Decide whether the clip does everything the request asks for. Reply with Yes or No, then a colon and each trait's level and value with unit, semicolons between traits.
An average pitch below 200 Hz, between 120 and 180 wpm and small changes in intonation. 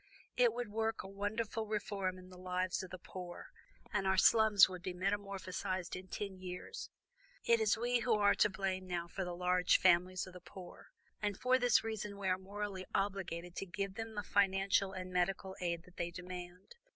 No: high, 190 Hz; average, 195 wpm; narrow, 2.2 semitones